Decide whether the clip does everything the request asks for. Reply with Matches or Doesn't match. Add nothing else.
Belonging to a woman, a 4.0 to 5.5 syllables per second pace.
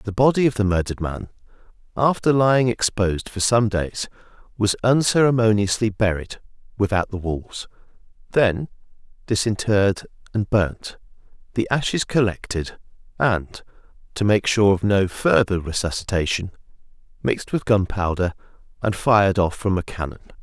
Doesn't match